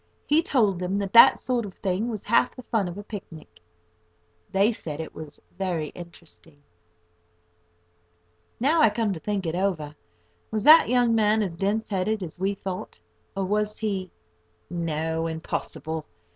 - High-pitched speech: Yes, high, 195 Hz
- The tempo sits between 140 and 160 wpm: Yes, average, 155 wpm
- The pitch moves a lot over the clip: No, average, 4.8 semitones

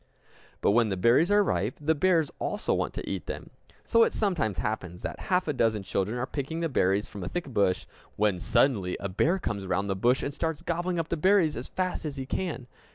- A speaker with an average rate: No, fast, 225 wpm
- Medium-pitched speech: No, low, 130 Hz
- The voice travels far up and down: Yes, wide, 8.8 semitones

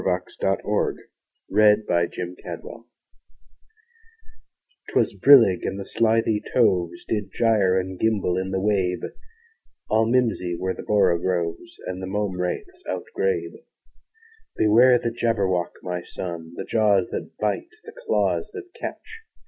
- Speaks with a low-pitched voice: Yes, low, 100 Hz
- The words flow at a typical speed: No, slow, 120 wpm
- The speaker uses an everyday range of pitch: Yes, average, 3.7 semitones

